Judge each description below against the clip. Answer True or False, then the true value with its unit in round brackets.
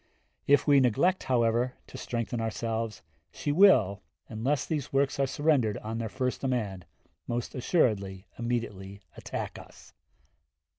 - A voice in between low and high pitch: False (120 Hz)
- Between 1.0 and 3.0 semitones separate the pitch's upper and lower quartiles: False (3.9 semitones)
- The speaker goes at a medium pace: False (130 wpm)